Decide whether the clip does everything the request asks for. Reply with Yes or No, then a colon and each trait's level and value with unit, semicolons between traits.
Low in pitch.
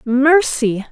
No: very high, 265 Hz